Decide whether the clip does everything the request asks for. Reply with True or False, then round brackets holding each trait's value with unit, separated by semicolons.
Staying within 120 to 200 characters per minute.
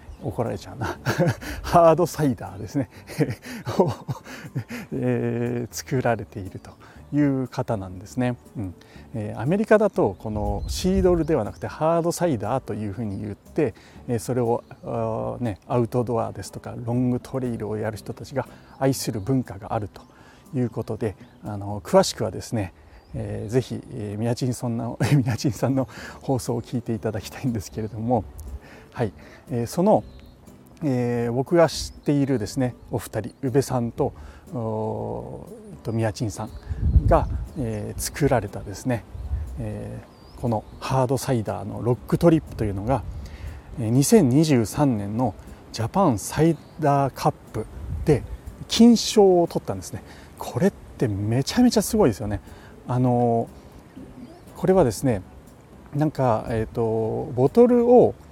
False (290 characters per minute)